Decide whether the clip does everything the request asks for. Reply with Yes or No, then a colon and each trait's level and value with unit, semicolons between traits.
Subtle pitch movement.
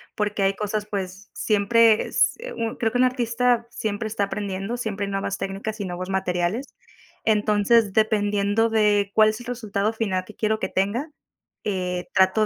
Yes: narrow, 2.3 semitones